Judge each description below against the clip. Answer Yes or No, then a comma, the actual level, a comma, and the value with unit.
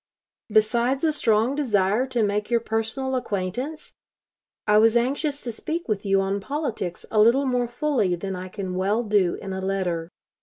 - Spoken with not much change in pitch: No, average, 4.6 semitones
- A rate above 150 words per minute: Yes, average, 175 wpm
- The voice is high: Yes, high, 220 Hz